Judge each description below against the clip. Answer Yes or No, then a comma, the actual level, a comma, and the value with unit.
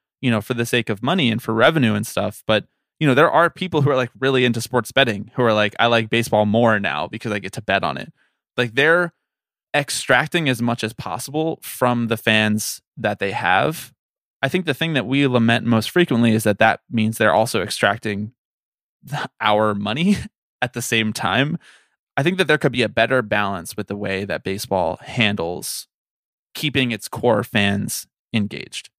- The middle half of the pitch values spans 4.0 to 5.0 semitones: No, average, 3.6 semitones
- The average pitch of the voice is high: No, low, 115 Hz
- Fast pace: No, average, 195 wpm